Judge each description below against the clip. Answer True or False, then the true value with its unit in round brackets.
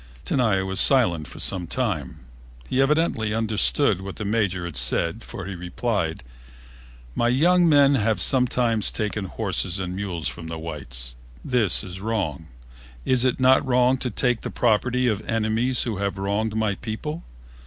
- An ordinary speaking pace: True (160 wpm)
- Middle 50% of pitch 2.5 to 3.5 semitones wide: False (5.1 semitones)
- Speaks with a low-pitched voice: True (110 Hz)